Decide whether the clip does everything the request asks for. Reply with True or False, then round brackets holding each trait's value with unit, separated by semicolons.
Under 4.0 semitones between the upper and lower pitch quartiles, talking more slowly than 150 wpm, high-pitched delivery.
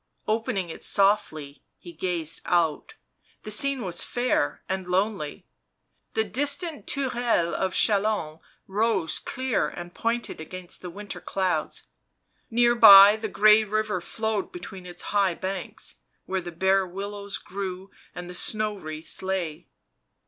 True (3.6 semitones; 140 wpm; 195 Hz)